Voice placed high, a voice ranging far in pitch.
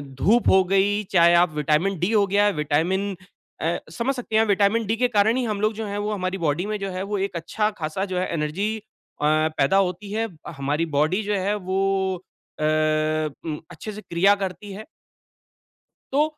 No: high, 195 Hz; average, 3.6 semitones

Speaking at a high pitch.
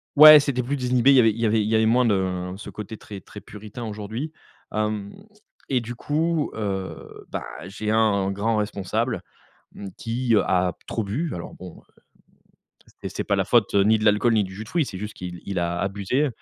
No: low, 105 Hz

